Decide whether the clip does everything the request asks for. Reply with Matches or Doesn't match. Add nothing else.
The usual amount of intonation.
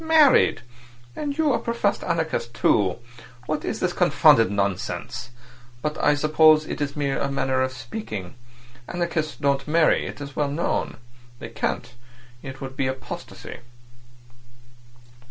Matches